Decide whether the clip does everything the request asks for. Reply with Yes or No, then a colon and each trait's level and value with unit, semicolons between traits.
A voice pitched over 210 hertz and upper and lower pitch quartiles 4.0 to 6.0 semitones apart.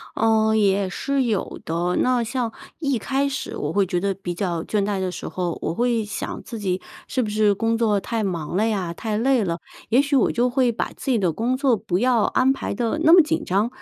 Yes: high, 220 Hz; average, 4.6 semitones